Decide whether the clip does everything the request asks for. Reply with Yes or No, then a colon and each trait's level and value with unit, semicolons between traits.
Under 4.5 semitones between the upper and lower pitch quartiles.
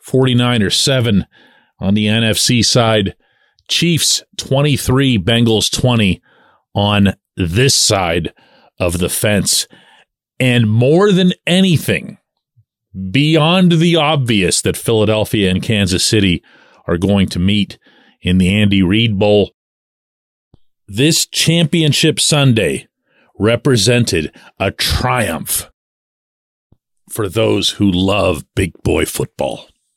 No: average, 5.1 semitones